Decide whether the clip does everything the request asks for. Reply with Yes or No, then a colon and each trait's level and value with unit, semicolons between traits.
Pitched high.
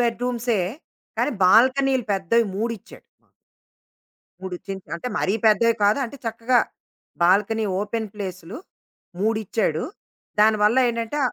Yes: high, 220 Hz